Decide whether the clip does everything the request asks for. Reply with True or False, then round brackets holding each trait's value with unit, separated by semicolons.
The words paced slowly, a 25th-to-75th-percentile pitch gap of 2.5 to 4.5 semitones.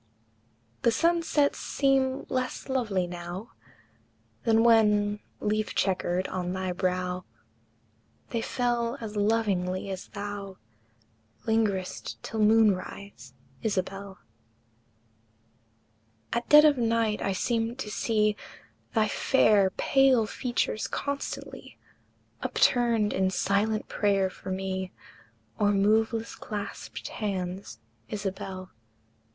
True (100 wpm; 3.3 semitones)